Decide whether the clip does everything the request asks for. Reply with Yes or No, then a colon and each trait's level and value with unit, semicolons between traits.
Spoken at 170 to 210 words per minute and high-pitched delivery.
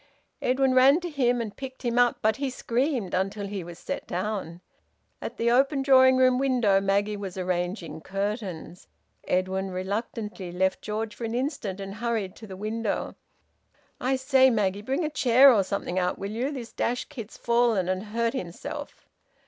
Yes: average, 175 wpm; high, 220 Hz